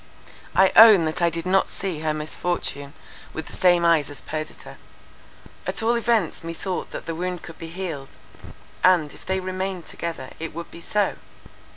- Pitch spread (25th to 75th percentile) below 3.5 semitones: Yes, average, 2.9 semitones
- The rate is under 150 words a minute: No, average, 175 wpm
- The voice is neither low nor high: Yes, medium, 170 Hz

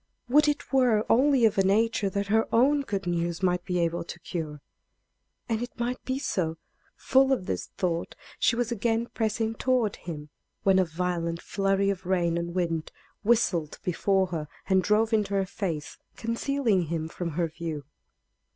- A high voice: Yes, high, 195 Hz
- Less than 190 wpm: Yes, average, 170 wpm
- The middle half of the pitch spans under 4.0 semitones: No, average, 5.0 semitones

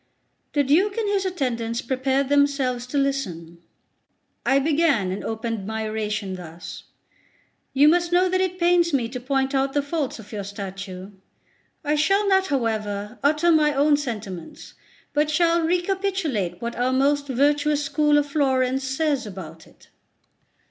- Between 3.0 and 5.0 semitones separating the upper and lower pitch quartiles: No, wide, 5.6 semitones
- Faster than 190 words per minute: No, average, 150 wpm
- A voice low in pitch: No, very high, 275 Hz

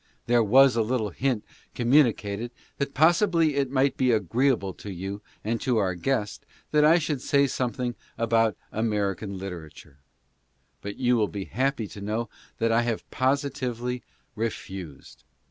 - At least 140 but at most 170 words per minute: Yes, average, 150 wpm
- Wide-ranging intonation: No, average, 4.5 semitones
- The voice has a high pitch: No, low, 120 Hz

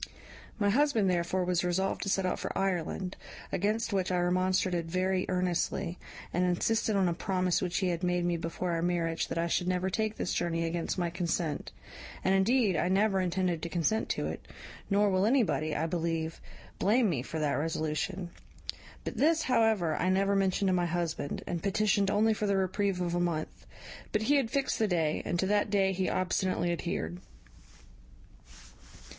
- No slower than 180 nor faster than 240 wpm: Yes, average, 185 wpm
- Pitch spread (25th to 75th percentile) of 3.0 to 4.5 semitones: No, narrow, 2.5 semitones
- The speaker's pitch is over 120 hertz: Yes, medium, 185 Hz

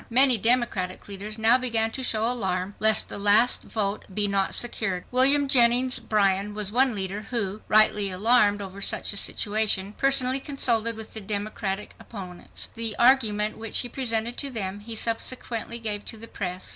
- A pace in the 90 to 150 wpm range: No, average, 170 wpm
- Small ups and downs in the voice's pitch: No, average, 3.0 semitones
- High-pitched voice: Yes, high, 220 Hz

